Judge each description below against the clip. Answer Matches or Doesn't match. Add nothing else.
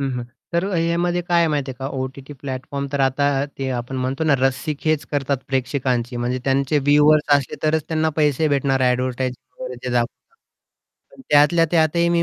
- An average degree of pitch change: Matches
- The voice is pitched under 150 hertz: Matches